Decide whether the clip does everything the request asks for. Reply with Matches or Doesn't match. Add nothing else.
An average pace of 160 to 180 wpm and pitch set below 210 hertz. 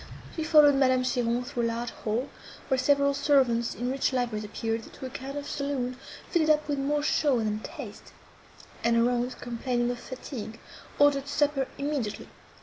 Doesn't match